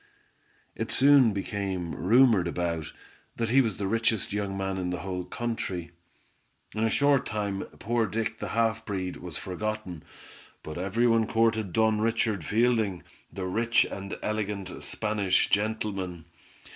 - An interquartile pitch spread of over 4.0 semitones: No, average, 3.4 semitones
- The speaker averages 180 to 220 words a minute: No, average, 145 wpm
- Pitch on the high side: No, low, 105 Hz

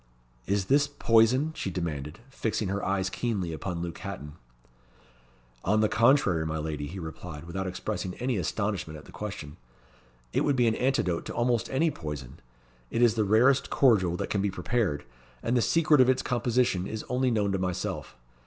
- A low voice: Yes, low, 100 Hz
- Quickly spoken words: No, average, 180 wpm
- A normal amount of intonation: No, wide, 6.0 semitones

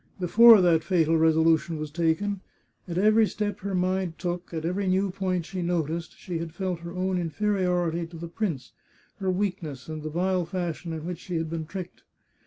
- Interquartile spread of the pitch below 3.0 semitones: Yes, narrow, 2.5 semitones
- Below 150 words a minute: No, average, 190 wpm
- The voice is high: No, medium, 175 Hz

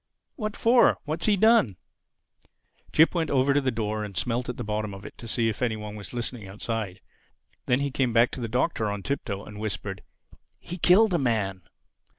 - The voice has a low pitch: Yes, low, 115 Hz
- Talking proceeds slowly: No, average, 195 wpm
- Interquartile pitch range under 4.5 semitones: No, average, 5.1 semitones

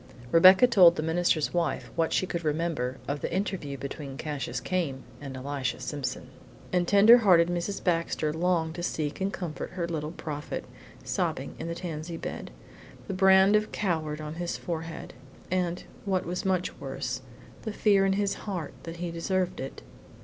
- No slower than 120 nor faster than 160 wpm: No, average, 170 wpm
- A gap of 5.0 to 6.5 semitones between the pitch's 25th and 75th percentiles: No, average, 3.4 semitones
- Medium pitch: Yes, medium, 170 Hz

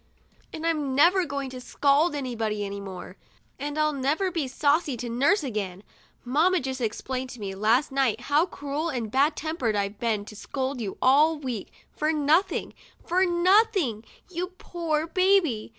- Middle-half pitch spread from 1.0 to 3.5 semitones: No, wide, 5.5 semitones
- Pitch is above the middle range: Yes, very high, 280 Hz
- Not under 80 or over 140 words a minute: No, average, 165 wpm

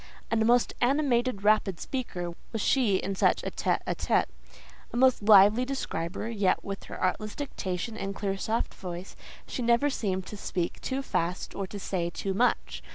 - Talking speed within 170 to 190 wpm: Yes, average, 175 wpm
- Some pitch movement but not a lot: Yes, average, 4.3 semitones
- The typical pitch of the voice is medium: No, high, 210 Hz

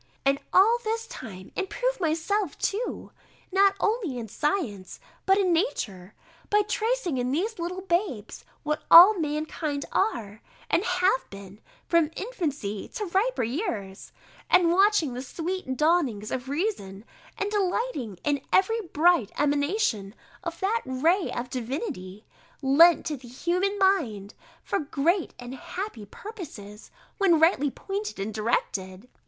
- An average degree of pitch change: No, wide, 8.2 semitones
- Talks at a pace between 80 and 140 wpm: Yes, slow, 135 wpm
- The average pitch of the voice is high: Yes, very high, 325 Hz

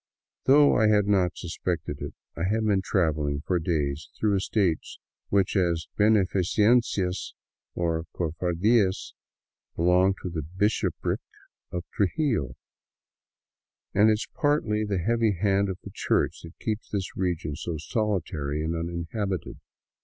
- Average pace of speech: No, slow, 130 wpm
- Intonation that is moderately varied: Yes, average, 4.1 semitones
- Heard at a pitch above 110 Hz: No, very low, 95 Hz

